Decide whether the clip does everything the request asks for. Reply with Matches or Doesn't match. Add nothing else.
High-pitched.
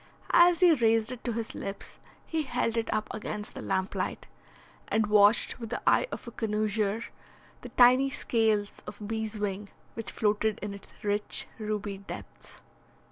Matches